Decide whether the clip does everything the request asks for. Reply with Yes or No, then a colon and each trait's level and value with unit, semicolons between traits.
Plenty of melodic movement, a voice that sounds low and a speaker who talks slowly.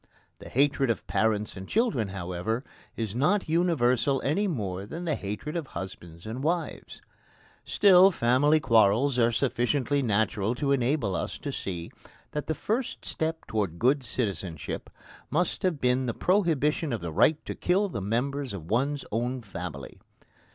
No: wide, 6.4 semitones; low, 125 Hz; average, 155 wpm